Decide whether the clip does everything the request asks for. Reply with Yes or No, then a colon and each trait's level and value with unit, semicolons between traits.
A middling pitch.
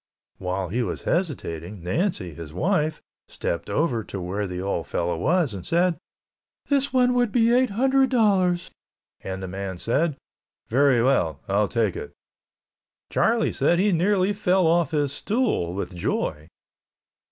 Yes: medium, 145 Hz